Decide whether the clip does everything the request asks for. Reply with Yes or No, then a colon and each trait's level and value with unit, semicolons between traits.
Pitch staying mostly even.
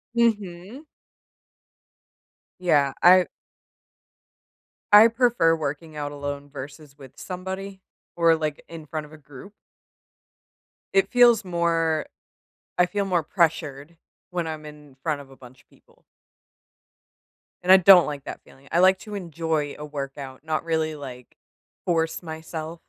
No: average, 3.8 semitones